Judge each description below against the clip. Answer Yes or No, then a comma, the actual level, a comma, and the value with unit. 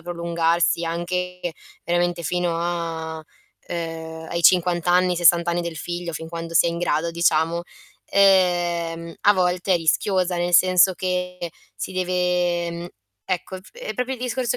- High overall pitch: No, medium, 175 Hz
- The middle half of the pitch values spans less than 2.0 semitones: Yes, narrow, 1.3 semitones